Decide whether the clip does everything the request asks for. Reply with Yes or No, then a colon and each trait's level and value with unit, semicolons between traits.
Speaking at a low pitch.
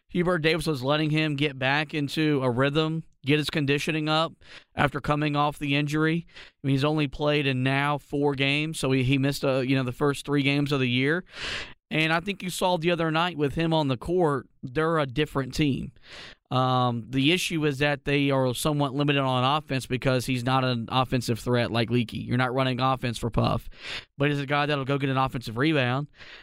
No: medium, 145 Hz